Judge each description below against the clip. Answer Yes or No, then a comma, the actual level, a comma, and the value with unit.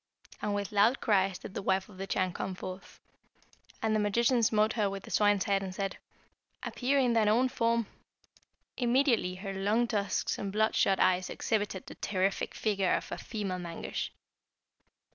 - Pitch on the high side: Yes, high, 205 Hz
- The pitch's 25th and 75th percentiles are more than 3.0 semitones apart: No, average, 2.7 semitones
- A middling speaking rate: Yes, average, 170 wpm